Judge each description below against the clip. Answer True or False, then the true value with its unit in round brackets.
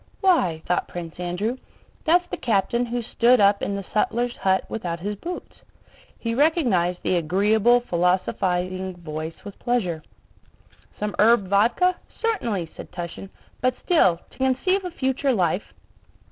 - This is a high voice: True (205 Hz)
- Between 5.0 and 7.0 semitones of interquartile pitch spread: True (5.5 semitones)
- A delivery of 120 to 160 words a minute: True (140 wpm)